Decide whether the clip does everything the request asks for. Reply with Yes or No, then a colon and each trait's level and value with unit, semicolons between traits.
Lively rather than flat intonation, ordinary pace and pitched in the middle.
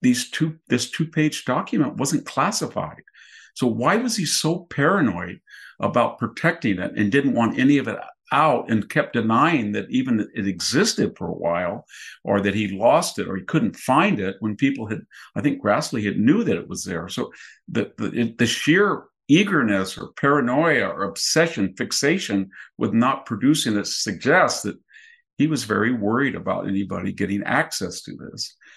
No: wide, 8.5 semitones; average, 175 wpm; low, 120 Hz